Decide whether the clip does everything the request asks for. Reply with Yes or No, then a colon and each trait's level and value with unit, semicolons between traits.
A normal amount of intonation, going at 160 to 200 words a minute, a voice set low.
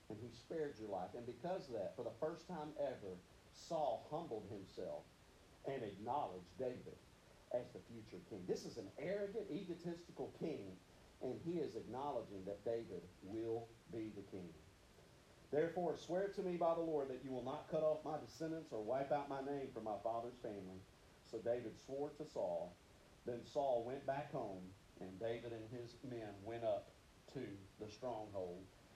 No: wide, 6.1 semitones; average, 175 wpm; low, 120 Hz